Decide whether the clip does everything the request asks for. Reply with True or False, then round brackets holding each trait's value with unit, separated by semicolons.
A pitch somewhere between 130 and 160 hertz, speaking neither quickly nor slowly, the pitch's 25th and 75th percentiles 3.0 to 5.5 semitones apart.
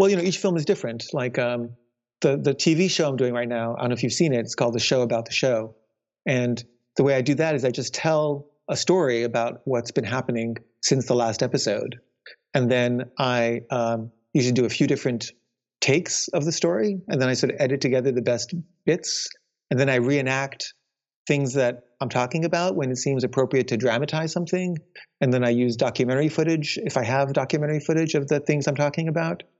False (135 Hz; 215 wpm; 3.9 semitones)